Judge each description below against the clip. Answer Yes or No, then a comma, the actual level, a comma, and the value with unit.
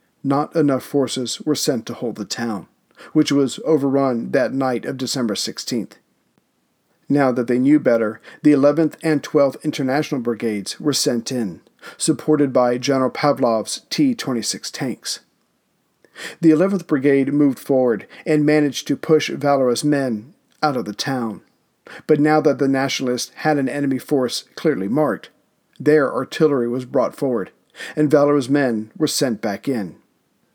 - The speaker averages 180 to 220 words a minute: No, average, 150 wpm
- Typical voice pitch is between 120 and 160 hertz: Yes, medium, 140 Hz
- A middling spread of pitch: Yes, average, 3.0 semitones